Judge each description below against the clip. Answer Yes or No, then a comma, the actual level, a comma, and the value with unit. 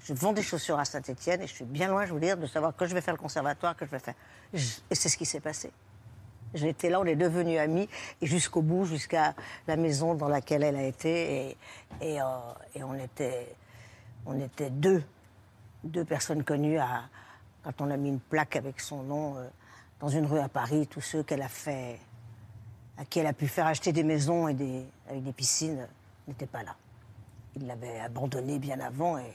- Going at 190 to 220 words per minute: Yes, average, 215 wpm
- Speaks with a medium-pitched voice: Yes, medium, 145 Hz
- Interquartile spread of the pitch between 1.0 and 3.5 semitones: No, average, 4.8 semitones